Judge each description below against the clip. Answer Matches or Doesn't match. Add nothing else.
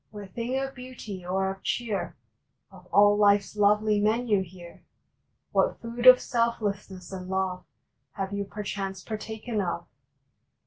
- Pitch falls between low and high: Doesn't match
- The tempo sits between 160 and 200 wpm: Doesn't match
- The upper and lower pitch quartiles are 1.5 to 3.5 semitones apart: Matches